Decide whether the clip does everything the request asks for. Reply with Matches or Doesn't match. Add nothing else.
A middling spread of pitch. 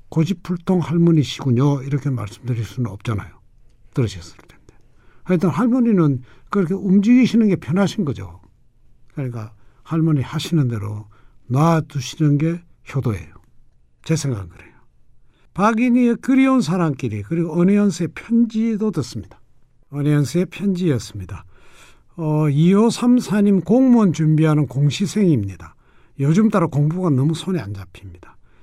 Doesn't match